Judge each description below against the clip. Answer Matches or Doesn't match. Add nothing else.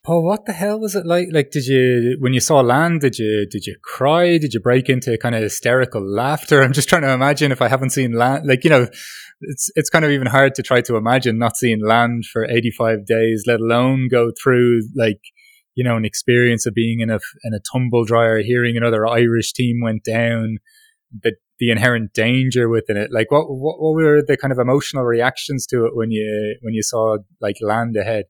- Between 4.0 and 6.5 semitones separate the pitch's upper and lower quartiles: Doesn't match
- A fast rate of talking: Matches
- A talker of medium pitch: Doesn't match